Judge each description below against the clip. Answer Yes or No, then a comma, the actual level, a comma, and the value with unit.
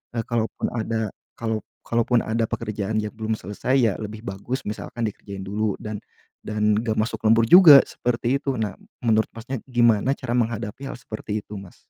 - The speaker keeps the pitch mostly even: Yes, narrow, 1.9 semitones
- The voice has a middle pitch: No, low, 110 Hz